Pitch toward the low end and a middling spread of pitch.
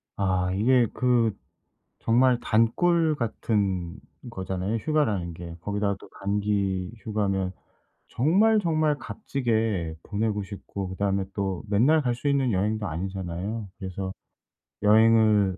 Yes: low, 105 Hz; average, 3.8 semitones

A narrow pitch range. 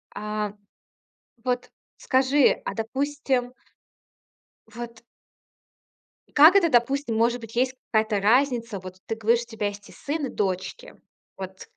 No: average, 3.8 semitones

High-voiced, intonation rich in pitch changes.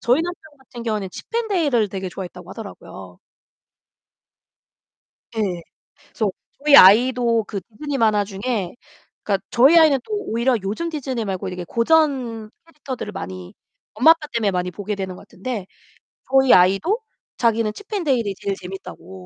Yes: high, 225 Hz; wide, 5.7 semitones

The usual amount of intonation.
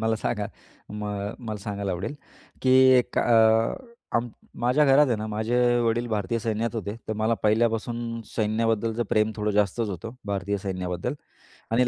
No: narrow, 2.0 semitones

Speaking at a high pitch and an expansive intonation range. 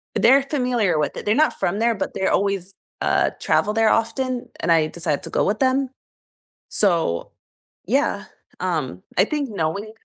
Yes: high, 210 Hz; wide, 6.2 semitones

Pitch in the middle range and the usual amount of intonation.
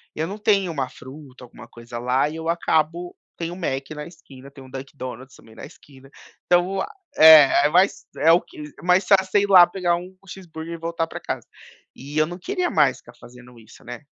Yes: medium, 160 Hz; average, 4.9 semitones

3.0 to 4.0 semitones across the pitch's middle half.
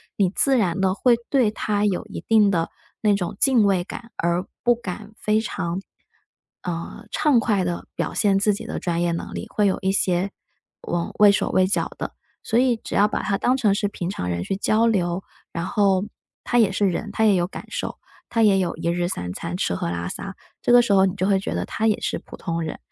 Yes: average, 3.5 semitones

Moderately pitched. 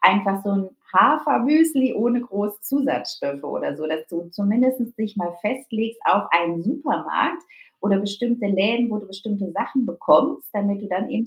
No: high, 210 Hz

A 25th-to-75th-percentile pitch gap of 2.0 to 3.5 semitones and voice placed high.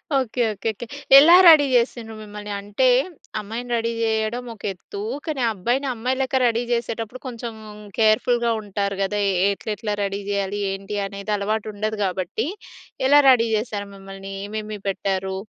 Yes: average, 3.1 semitones; high, 215 Hz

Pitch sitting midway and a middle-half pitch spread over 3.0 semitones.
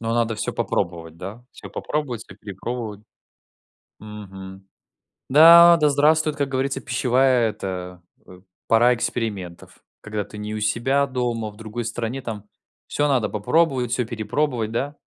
No: low, 115 Hz; average, 4.2 semitones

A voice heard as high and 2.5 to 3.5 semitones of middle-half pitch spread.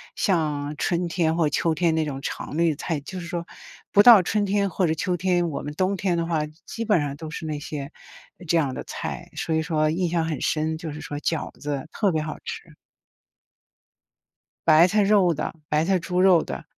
No: medium, 165 Hz; average, 2.9 semitones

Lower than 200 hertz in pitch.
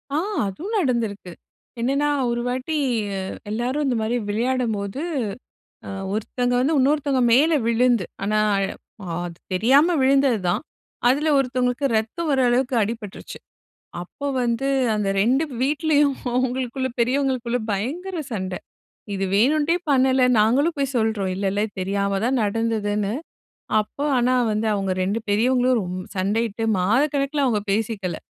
No: high, 245 Hz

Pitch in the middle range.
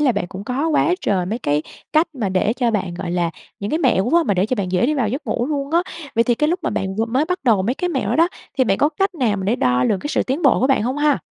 No: high, 245 Hz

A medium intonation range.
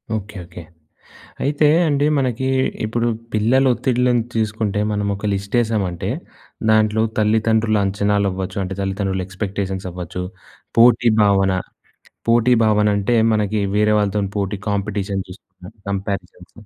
No: narrow, 2.3 semitones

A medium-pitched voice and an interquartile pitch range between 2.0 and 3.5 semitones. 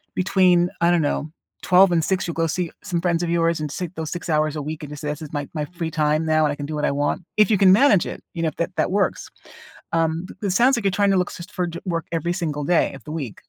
Yes: medium, 165 Hz; average, 2.8 semitones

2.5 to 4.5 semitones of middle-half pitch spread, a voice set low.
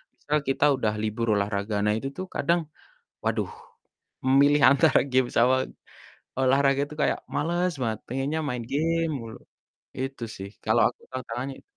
Yes: average, 4.0 semitones; low, 130 Hz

